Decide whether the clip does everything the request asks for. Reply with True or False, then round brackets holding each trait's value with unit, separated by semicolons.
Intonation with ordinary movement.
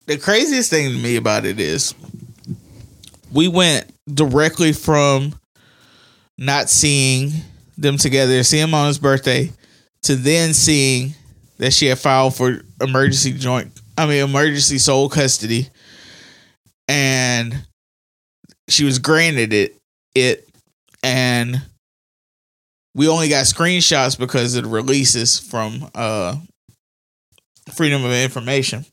True (3.2 semitones)